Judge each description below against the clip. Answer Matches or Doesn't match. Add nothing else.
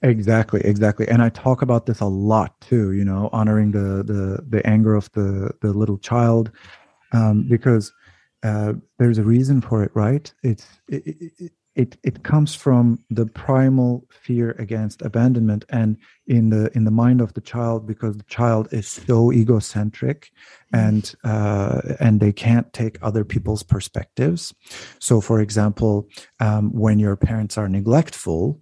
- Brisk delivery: Doesn't match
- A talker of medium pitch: Doesn't match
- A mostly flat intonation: Matches